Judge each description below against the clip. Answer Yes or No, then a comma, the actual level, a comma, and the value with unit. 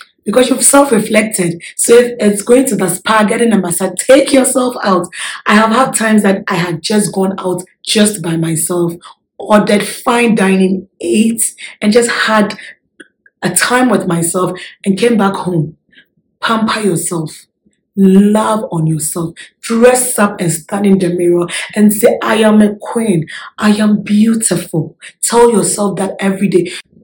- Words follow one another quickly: No, average, 160 wpm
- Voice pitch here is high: Yes, high, 205 Hz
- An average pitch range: Yes, average, 3.6 semitones